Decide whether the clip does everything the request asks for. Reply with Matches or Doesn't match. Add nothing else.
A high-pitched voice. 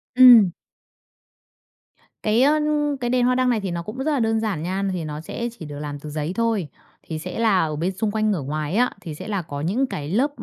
Matches